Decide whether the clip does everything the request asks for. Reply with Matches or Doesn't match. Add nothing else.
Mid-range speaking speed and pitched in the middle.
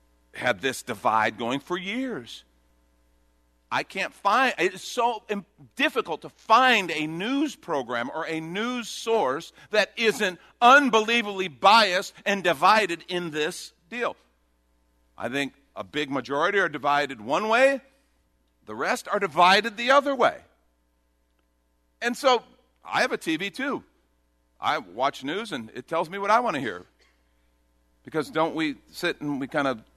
Matches